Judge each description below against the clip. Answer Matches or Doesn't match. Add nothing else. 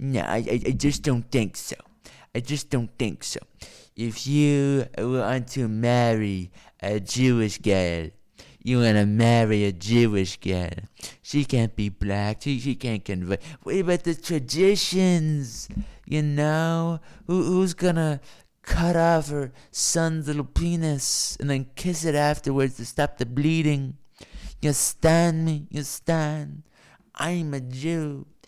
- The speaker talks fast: Doesn't match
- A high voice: Doesn't match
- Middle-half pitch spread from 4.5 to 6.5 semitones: Matches